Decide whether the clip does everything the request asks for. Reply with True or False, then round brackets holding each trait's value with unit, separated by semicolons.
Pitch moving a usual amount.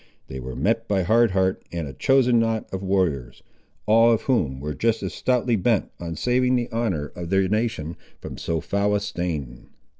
False (5.9 semitones)